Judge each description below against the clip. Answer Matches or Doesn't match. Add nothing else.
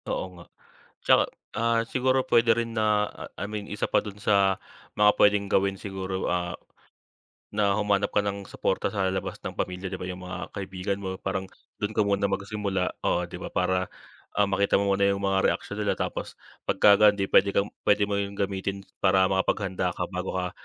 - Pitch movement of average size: Doesn't match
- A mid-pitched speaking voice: Doesn't match